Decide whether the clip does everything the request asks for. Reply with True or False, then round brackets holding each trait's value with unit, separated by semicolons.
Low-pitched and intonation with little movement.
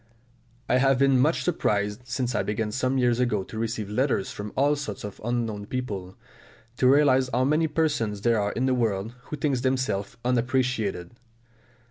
False (125 Hz; 3.9 semitones)